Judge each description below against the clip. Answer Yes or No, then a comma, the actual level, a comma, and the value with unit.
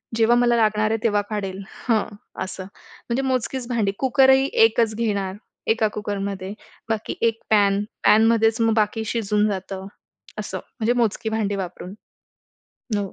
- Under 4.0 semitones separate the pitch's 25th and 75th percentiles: Yes, narrow, 2.4 semitones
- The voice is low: No, high, 220 Hz